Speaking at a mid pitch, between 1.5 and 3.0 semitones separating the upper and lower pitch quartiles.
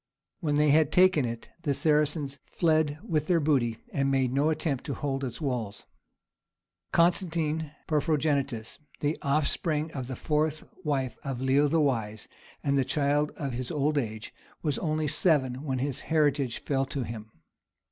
Yes: medium, 145 Hz; average, 2.7 semitones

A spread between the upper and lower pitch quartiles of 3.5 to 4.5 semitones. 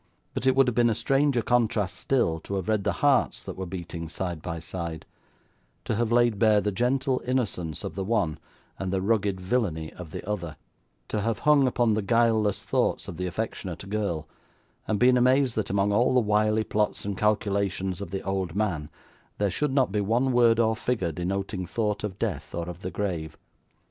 Yes: average, 4.2 semitones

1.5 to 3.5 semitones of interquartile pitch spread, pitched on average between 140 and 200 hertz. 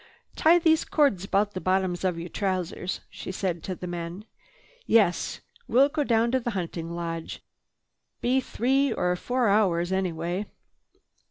No: average, 5.3 semitones; high, 190 Hz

